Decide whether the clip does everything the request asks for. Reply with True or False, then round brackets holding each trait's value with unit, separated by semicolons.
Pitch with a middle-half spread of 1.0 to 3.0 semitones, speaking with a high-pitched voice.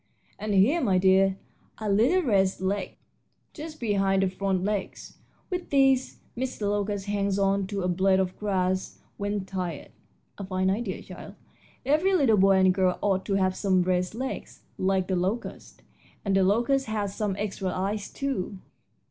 True (2.4 semitones; 195 Hz)